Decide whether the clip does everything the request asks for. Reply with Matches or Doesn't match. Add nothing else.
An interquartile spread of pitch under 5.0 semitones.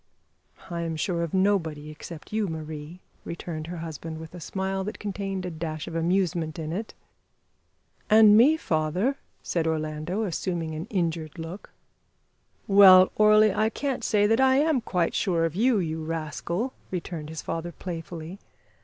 Matches